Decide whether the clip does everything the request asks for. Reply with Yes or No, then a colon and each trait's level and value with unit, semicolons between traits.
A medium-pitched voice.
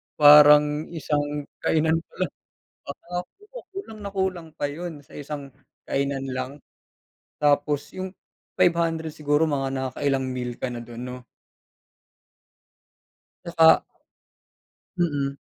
Yes: medium, 150 Hz